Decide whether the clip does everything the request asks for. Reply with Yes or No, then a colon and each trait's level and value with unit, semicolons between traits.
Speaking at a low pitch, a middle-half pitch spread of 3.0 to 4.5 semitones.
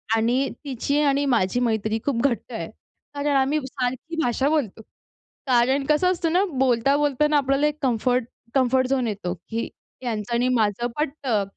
No: very high, 260 Hz; average, 3.5 semitones